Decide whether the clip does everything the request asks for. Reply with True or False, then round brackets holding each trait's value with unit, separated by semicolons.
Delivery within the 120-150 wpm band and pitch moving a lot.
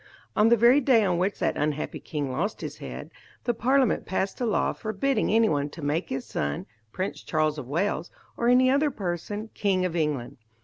False (190 wpm; 7.2 semitones)